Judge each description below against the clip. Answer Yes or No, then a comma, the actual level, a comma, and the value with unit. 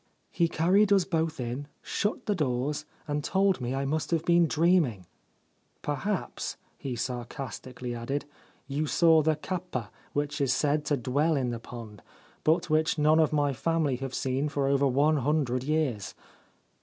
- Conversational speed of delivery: Yes, average, 170 wpm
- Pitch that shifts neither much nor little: Yes, average, 3.8 semitones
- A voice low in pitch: No, medium, 145 Hz